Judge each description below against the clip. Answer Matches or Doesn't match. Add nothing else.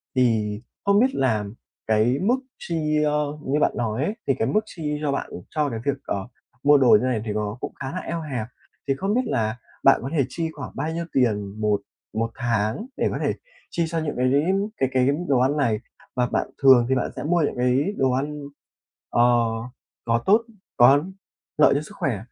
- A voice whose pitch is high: Doesn't match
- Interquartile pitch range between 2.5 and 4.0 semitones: Doesn't match